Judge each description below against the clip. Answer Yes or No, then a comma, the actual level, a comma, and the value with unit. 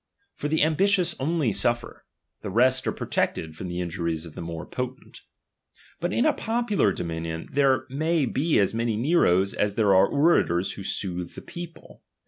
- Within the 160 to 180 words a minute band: No, average, 195 wpm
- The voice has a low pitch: Yes, low, 115 Hz